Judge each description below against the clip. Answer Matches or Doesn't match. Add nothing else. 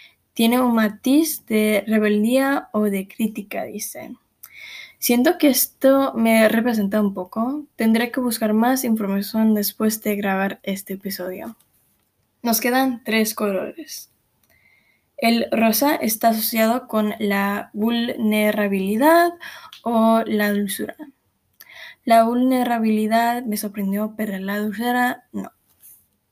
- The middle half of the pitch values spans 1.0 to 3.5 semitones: Matches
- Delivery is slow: Matches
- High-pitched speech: Matches